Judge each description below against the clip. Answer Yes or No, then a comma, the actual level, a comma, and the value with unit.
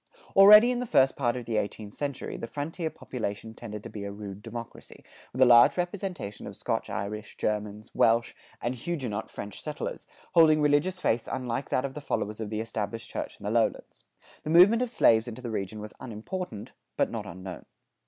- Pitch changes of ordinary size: No, wide, 6.0 semitones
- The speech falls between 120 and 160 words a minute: No, average, 190 wpm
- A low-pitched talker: Yes, low, 120 Hz